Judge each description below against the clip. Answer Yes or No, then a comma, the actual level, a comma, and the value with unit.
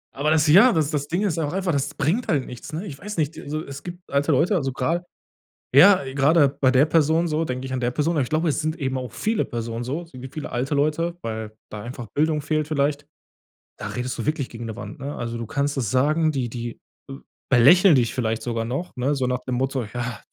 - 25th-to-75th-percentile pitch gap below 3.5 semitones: No, average, 3.9 semitones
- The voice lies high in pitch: No, medium, 140 Hz